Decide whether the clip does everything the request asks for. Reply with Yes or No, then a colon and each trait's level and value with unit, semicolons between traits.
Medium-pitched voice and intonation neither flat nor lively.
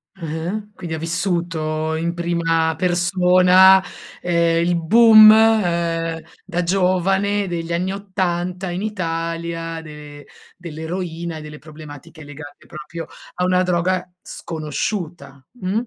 No: medium, 170 Hz; narrow, 2.1 semitones